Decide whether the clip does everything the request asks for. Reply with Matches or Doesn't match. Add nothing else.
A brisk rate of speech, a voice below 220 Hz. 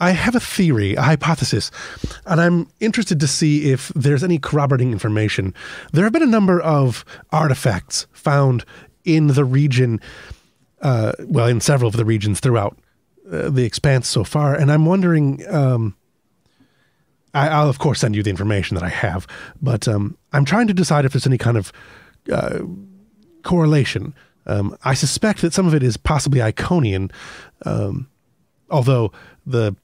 Doesn't match